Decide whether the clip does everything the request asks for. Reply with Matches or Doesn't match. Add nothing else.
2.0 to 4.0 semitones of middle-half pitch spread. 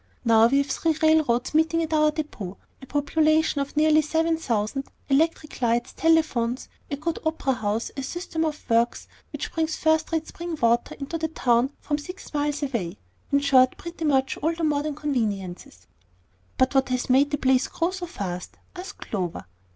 Doesn't match